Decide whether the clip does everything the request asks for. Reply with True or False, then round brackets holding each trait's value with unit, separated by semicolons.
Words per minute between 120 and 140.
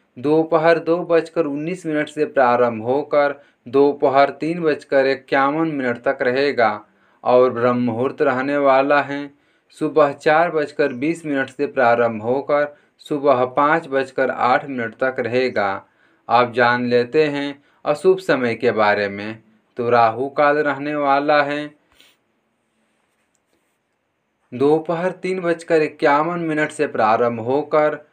True (125 wpm)